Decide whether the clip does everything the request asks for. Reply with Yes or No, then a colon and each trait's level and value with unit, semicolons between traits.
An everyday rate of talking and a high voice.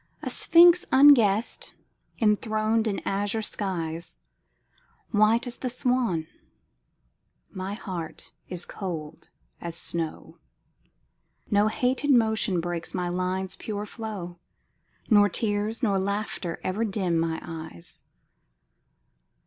No: slow, 100 wpm; high, 205 Hz